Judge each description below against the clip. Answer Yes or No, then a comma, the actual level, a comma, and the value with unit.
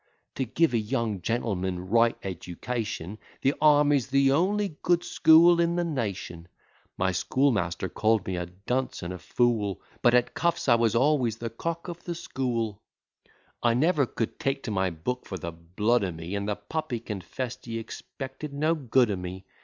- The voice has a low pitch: Yes, low, 115 Hz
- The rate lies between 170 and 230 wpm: Yes, average, 175 wpm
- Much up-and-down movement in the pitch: Yes, wide, 6.4 semitones